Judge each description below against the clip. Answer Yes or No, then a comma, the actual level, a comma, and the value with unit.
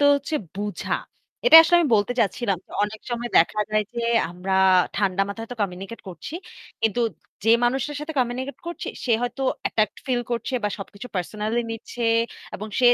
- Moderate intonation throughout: Yes, average, 3.6 semitones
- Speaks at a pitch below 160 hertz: No, high, 225 Hz